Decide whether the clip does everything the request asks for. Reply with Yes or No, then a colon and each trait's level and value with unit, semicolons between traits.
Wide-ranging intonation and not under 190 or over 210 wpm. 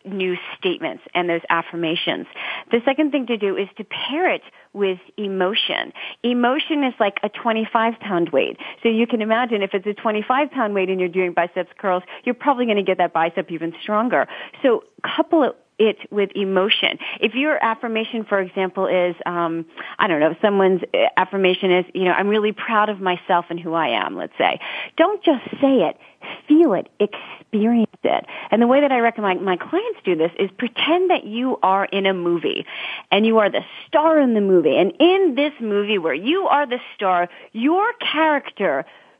Yes: wide, 7.1 semitones; average, 195 wpm